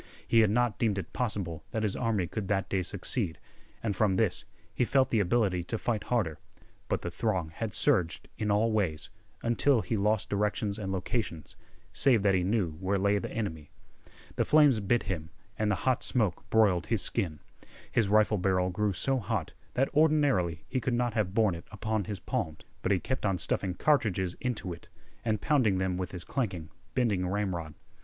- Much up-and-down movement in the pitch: No, average, 3.9 semitones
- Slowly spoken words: No, average, 190 wpm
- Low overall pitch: Yes, low, 105 Hz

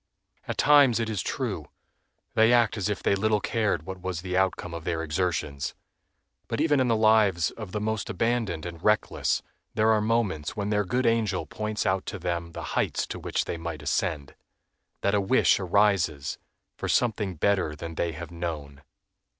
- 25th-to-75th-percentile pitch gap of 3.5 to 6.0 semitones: Yes, average, 4.4 semitones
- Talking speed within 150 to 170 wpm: No, average, 185 wpm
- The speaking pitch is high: No, very low, 95 Hz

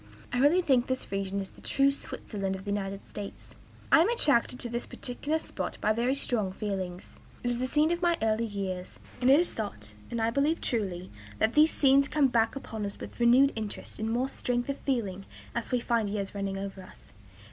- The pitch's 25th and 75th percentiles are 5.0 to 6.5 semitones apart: Yes, average, 5.3 semitones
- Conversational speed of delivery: No, fast, 210 wpm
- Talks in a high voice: Yes, high, 235 Hz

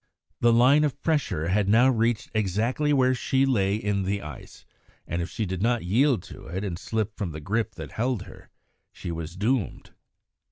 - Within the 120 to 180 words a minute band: No, average, 190 wpm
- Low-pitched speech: Yes, low, 110 Hz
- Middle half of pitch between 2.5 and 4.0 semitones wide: No, average, 4.8 semitones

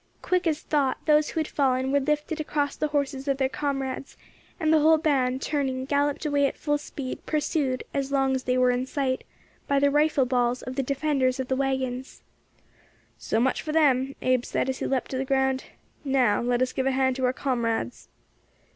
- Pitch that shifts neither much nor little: No, narrow, 2.1 semitones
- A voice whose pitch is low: No, very high, 270 Hz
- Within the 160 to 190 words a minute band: No, fast, 205 wpm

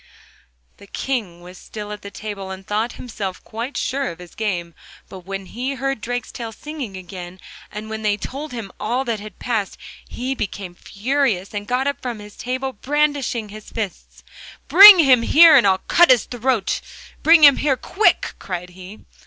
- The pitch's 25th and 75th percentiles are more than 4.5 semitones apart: Yes, average, 5.2 semitones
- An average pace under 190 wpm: Yes, average, 170 wpm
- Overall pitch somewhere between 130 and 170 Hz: No, high, 220 Hz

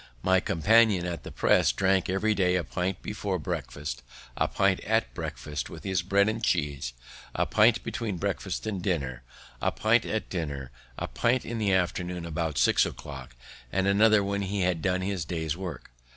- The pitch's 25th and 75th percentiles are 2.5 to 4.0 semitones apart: Yes, average, 3.5 semitones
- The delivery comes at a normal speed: Yes, average, 180 wpm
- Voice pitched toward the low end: Yes, very low, 95 Hz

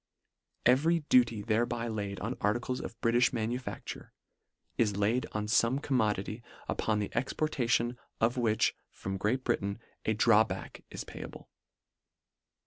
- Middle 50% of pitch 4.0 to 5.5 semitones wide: No, average, 2.8 semitones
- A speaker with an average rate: No, slow, 130 wpm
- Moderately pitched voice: No, low, 115 Hz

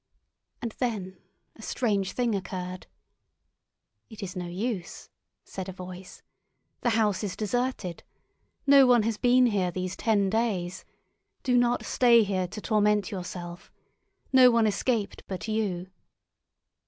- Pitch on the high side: Yes, high, 205 Hz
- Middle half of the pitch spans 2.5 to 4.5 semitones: Yes, average, 4.2 semitones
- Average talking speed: No, slow, 130 wpm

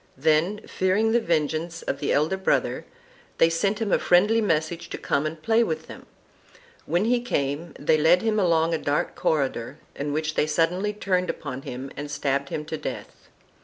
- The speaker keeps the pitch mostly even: No, average, 4.3 semitones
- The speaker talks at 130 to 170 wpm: No, average, 185 wpm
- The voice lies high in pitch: No, medium, 165 Hz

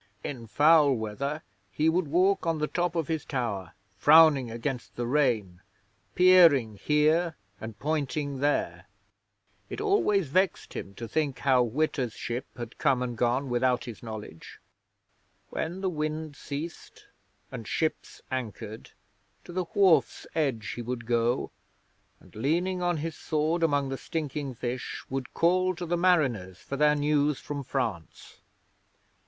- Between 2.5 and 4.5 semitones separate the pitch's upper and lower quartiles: No, average, 5.0 semitones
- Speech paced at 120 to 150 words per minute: Yes, average, 145 wpm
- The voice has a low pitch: No, medium, 145 Hz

